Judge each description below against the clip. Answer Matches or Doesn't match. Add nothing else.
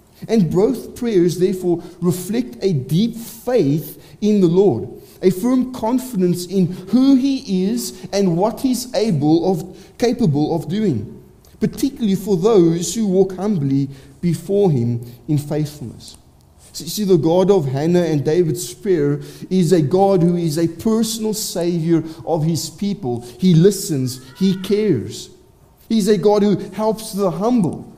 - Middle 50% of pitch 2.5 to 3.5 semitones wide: Doesn't match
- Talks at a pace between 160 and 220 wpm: Doesn't match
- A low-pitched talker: Doesn't match